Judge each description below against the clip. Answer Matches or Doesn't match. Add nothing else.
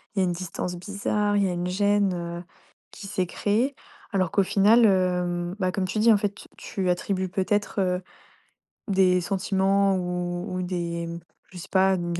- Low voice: Doesn't match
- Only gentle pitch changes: Matches